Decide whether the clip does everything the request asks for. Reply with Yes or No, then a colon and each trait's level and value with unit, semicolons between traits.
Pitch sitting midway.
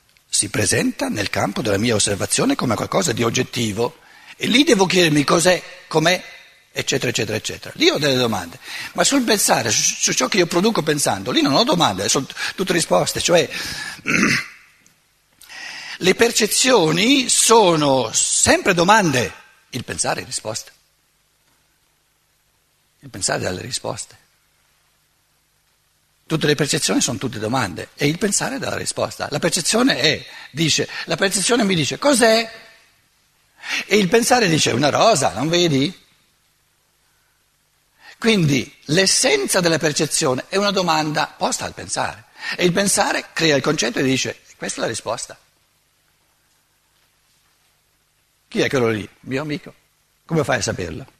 Yes: medium, 170 Hz